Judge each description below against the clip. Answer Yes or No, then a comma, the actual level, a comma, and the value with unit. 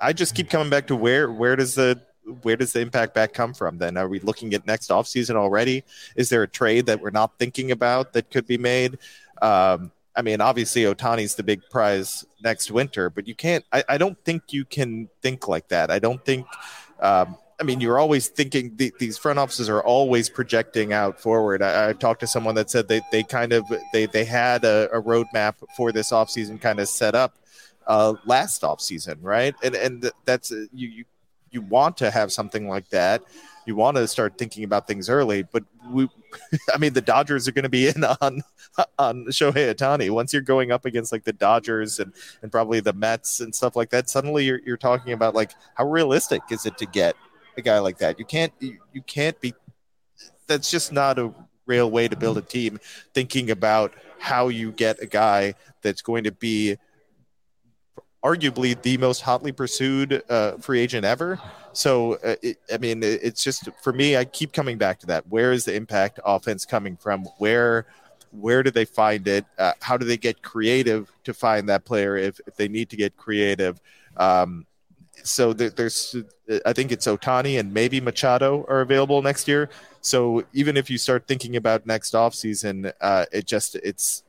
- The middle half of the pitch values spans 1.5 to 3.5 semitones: Yes, average, 3.1 semitones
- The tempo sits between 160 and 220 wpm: Yes, fast, 205 wpm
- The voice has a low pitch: Yes, low, 120 Hz